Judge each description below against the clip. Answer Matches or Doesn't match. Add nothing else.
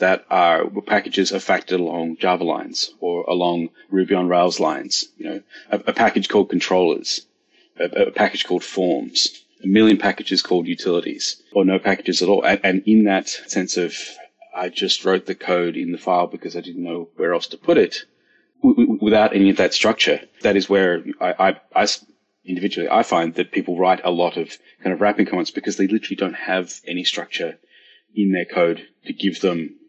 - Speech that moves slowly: Doesn't match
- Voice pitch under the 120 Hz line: Matches